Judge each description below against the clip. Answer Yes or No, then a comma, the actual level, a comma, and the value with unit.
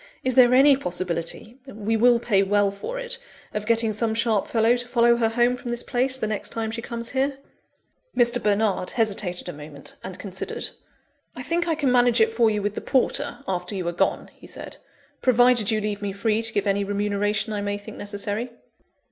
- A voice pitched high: Yes, high, 220 Hz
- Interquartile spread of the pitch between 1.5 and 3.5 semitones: Yes, average, 3.1 semitones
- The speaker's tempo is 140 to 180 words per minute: No, fast, 205 wpm